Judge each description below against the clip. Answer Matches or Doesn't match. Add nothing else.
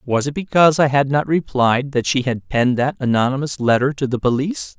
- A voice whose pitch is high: Doesn't match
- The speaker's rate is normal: Doesn't match